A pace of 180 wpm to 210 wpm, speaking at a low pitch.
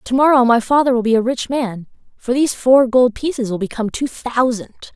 No: fast, 205 wpm; high, 245 Hz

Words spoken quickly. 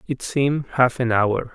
No: average, 195 wpm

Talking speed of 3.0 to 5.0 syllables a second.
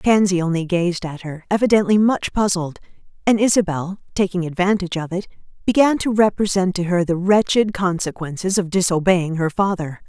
No: 5.4 syllables/s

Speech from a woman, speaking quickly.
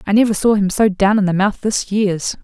Yes: female; fast, 270 wpm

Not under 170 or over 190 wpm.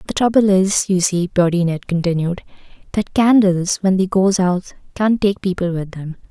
Yes: average, 180 wpm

